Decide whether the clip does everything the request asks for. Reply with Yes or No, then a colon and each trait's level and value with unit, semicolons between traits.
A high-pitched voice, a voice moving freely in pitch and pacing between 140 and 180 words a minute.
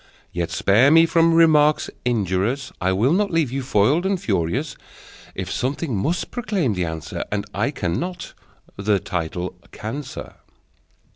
No: low, 130 Hz; wide, 8.7 semitones; average, 145 wpm